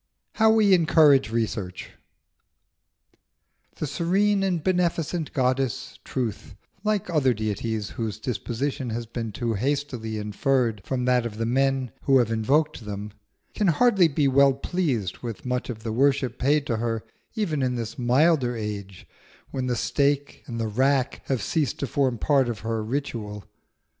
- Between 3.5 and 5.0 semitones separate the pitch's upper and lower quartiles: Yes, average, 4.3 semitones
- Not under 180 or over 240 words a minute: No, average, 155 wpm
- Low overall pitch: Yes, low, 130 Hz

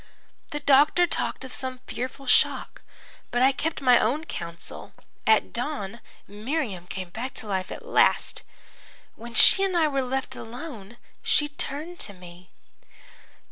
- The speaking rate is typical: Yes, average, 145 wpm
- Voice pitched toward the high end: Yes, very high, 255 Hz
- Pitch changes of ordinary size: No, wide, 5.7 semitones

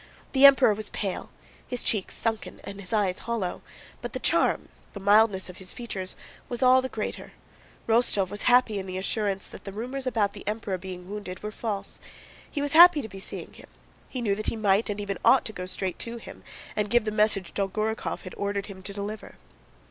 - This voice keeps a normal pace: No, fast, 210 wpm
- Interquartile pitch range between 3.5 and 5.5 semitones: No, average, 2.9 semitones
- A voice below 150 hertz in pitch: No, high, 210 Hz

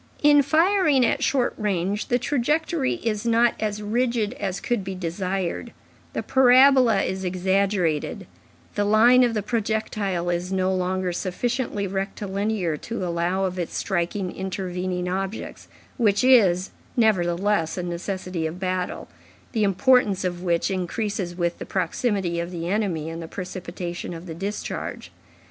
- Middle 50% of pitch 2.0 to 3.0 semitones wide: No, average, 3.9 semitones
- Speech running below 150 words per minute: Yes, average, 140 wpm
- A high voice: Yes, high, 195 Hz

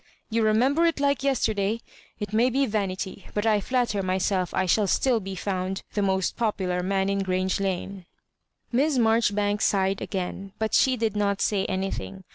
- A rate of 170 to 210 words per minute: Yes, average, 180 wpm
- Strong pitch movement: No, average, 3.0 semitones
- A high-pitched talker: Yes, high, 200 Hz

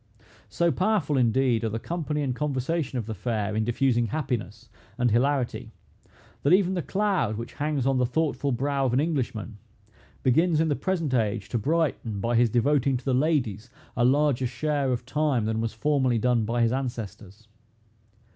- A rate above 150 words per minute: Yes, average, 175 wpm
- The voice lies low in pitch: Yes, low, 130 Hz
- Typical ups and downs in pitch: Yes, average, 4.4 semitones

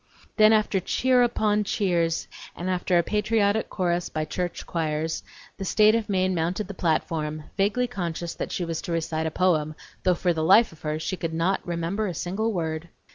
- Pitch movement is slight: No, average, 4.1 semitones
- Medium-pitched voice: Yes, medium, 180 Hz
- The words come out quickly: No, average, 195 wpm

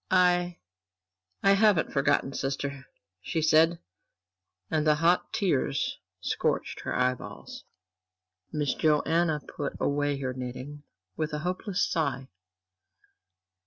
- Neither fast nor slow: No, slow, 105 wpm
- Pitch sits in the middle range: Yes, medium, 150 Hz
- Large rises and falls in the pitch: No, average, 3.8 semitones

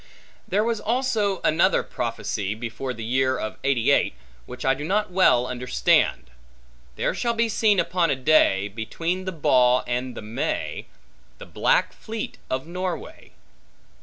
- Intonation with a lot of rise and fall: Yes, wide, 8.5 semitones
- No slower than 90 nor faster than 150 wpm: Yes, average, 145 wpm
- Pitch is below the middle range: No, medium, 145 Hz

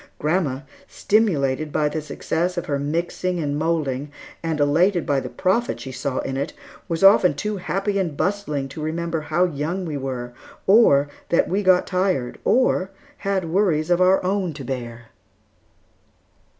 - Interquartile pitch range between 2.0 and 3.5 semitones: No, average, 4.6 semitones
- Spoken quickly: No, average, 160 wpm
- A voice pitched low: No, medium, 165 Hz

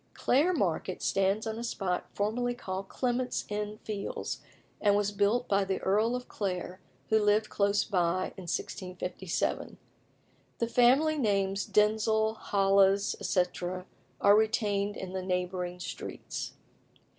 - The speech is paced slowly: Yes, slow, 130 wpm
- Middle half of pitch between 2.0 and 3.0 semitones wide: Yes, narrow, 2.6 semitones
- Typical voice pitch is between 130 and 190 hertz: No, high, 200 Hz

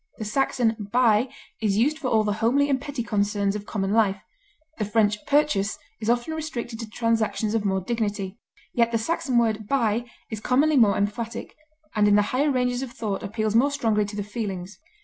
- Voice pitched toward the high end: Yes, high, 225 Hz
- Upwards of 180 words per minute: Yes, average, 190 wpm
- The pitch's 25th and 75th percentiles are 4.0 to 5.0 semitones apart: No, average, 3.0 semitones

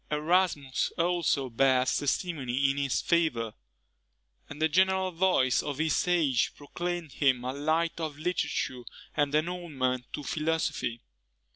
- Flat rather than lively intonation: No, average, 4.3 semitones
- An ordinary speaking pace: No, slow, 130 wpm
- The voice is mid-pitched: Yes, medium, 150 Hz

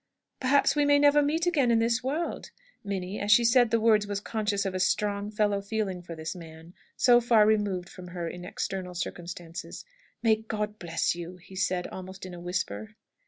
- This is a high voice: Yes, high, 205 Hz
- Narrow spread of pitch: No, average, 4.2 semitones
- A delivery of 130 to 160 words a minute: No, average, 195 wpm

